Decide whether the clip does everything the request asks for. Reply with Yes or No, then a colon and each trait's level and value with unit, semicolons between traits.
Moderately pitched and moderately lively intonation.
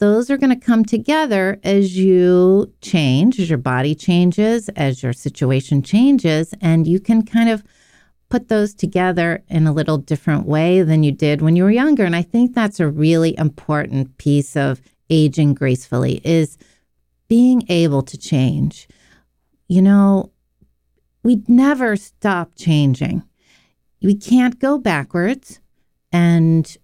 No: medium, 175 Hz; wide, 5.9 semitones